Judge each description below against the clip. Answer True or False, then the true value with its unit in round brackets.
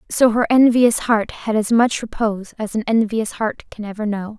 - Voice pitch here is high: True (220 Hz)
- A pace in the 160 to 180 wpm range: False (205 wpm)